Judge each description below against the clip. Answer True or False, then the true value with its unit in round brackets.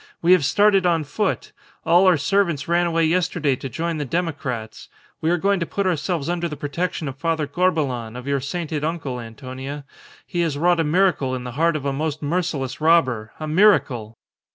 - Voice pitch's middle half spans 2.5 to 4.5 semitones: True (4.1 semitones)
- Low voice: False (155 Hz)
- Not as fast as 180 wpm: False (195 wpm)